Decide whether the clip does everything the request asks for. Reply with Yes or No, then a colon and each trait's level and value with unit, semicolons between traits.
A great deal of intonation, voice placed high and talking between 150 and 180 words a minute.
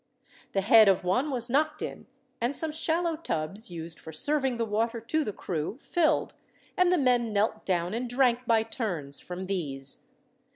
Yes: wide, 6.8 semitones; high, 230 Hz; average, 175 wpm